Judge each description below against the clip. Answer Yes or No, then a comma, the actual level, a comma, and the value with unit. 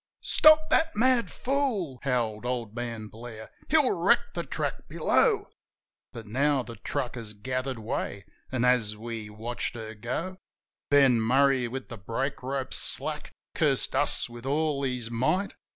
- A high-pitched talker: No, low, 125 Hz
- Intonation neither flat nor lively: Yes, average, 4.2 semitones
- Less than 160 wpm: Yes, average, 150 wpm